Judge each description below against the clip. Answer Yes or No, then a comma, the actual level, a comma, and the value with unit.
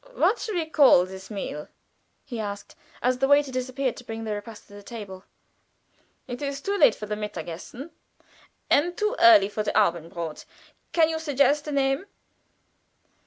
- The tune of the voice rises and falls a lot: Yes, wide, 5.9 semitones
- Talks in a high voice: Yes, high, 245 Hz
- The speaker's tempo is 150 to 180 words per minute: Yes, average, 165 wpm